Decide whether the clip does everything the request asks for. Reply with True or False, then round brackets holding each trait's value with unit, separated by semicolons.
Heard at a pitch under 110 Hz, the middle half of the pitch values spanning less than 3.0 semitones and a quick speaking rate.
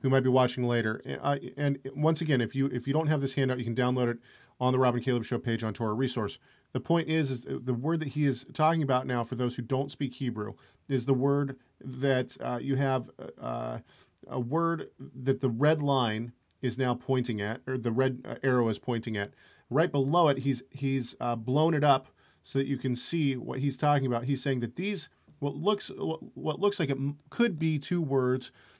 False (130 Hz; 2.6 semitones; 220 wpm)